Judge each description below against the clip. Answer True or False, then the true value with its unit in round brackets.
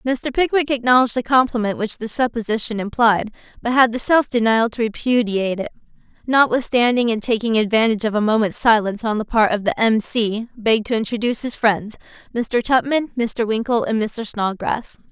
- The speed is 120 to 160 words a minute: False (175 wpm)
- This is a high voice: True (230 Hz)